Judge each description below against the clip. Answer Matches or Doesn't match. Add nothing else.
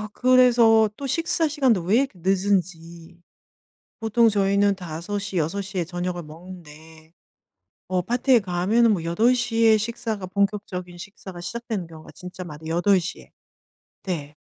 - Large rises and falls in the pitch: Doesn't match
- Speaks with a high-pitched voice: Matches